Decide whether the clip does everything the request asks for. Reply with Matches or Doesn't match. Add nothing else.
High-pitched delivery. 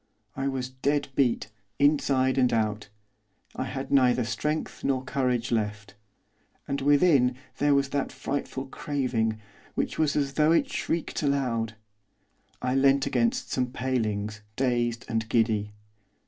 Doesn't match